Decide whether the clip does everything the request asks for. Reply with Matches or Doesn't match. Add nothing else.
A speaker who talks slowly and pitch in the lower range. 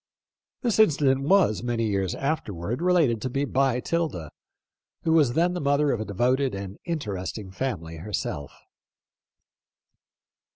Matches